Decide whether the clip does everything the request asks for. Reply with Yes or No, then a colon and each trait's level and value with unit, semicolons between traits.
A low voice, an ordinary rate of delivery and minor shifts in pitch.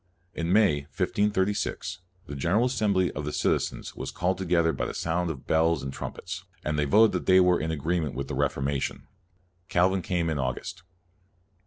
No: very low, 85 Hz; average, 190 wpm; average, 4.0 semitones